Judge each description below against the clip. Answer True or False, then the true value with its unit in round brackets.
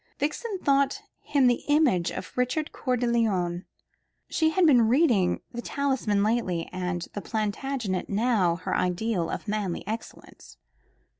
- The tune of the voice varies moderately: False (6.6 semitones)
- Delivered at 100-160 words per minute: True (140 wpm)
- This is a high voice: True (230 Hz)